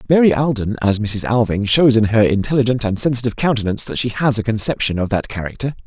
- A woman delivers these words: No, male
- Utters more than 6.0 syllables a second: Yes, 6.5 syllables/s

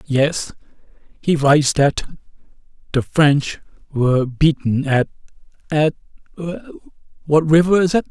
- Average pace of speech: No, slow, 105 wpm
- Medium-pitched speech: Yes, medium, 150 Hz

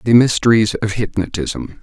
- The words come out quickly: No, slow, 130 wpm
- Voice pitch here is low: Yes, low, 105 Hz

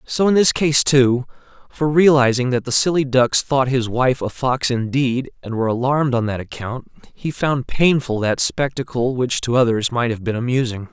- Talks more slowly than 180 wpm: No, average, 190 wpm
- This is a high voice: No, low, 130 Hz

